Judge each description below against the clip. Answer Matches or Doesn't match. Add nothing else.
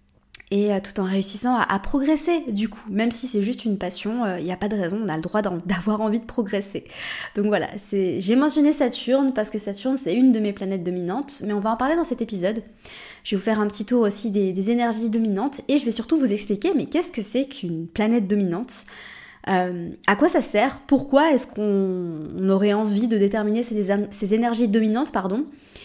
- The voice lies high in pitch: Matches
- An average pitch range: Matches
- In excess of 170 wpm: Matches